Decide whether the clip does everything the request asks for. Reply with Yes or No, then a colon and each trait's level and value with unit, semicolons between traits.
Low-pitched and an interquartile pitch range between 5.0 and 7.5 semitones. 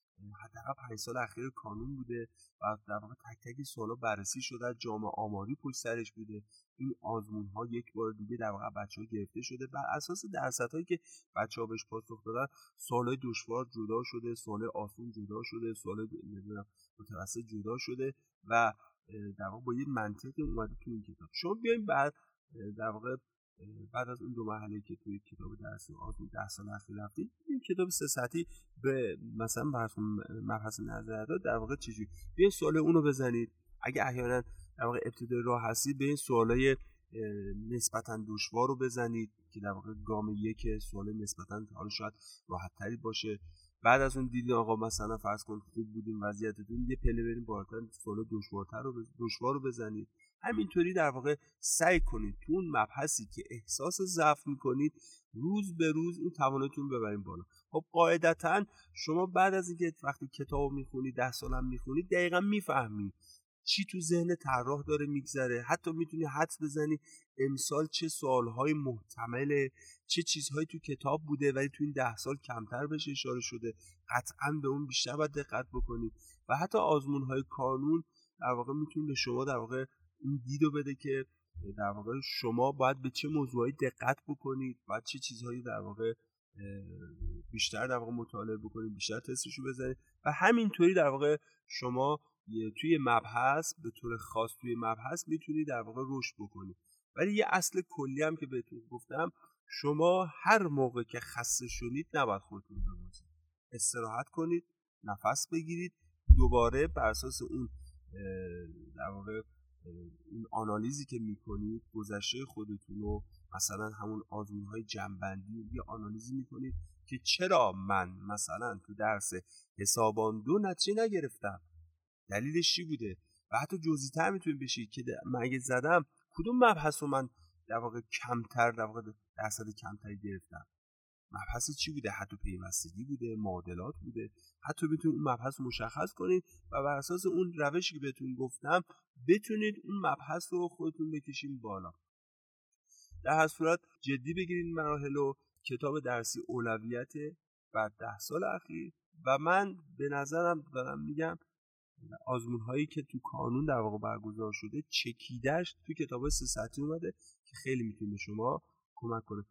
Yes: low, 120 Hz; wide, 5.6 semitones